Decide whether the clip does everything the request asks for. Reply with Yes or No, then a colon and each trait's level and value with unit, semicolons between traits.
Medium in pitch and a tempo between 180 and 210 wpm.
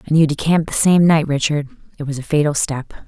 No: medium, 150 Hz; fast, 235 wpm